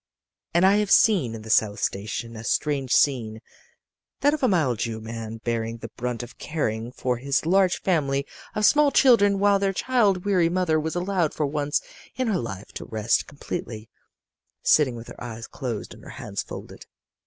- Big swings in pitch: Yes, wide, 8.5 semitones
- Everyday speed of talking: Yes, average, 185 wpm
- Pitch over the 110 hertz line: Yes, medium, 140 Hz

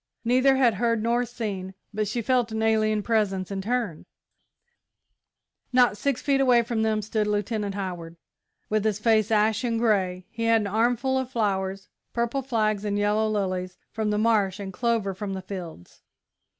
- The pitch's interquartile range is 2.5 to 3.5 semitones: Yes, average, 2.8 semitones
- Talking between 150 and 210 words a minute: Yes, average, 165 wpm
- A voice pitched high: Yes, high, 215 Hz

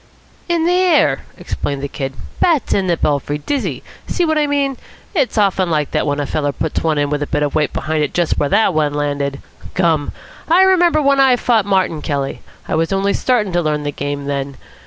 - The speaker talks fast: Yes, fast, 220 wpm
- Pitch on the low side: No, medium, 165 Hz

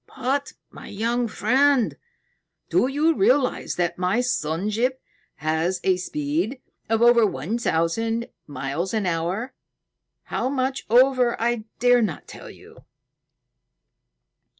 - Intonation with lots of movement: Yes, wide, 5.9 semitones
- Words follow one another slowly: Yes, slow, 120 wpm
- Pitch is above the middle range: Yes, high, 230 Hz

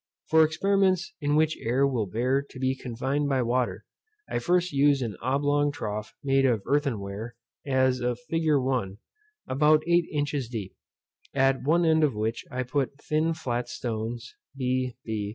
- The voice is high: No, low, 135 Hz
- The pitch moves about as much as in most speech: Yes, average, 3.5 semitones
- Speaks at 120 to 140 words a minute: No, average, 165 wpm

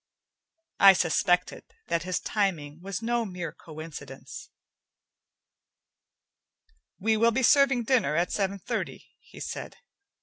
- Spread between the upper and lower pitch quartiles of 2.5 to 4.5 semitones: No, average, 5.2 semitones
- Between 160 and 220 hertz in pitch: Yes, high, 190 Hz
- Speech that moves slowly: Yes, slow, 110 wpm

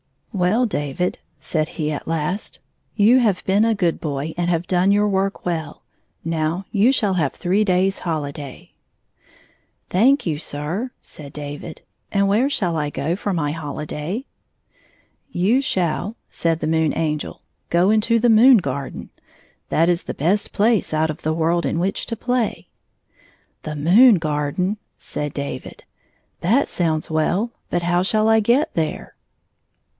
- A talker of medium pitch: Yes, medium, 175 Hz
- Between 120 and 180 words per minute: Yes, average, 160 wpm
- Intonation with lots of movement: No, average, 5.0 semitones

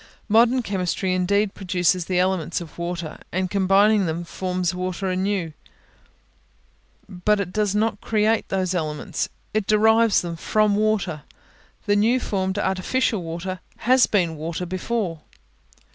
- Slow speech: Yes, slow, 130 wpm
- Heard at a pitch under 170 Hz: No, high, 190 Hz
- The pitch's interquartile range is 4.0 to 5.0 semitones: No, average, 3.0 semitones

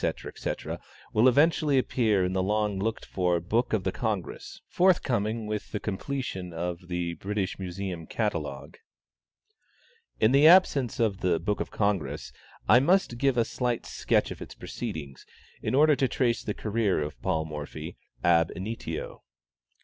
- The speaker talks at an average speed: Yes, average, 155 wpm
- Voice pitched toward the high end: No, low, 105 Hz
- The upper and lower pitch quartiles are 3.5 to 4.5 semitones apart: No, average, 5.3 semitones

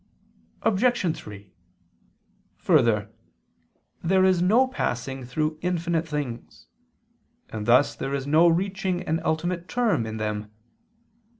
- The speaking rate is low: Yes, slow, 110 wpm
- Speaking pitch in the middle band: Yes, medium, 160 Hz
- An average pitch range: No, wide, 6.9 semitones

